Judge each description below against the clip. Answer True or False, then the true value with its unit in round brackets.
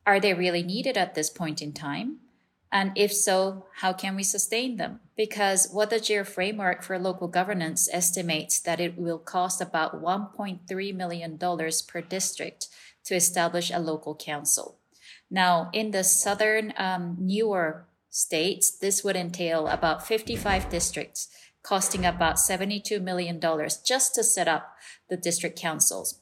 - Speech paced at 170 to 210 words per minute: False (145 wpm)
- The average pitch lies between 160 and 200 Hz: True (185 Hz)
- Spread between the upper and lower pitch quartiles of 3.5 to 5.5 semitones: False (2.9 semitones)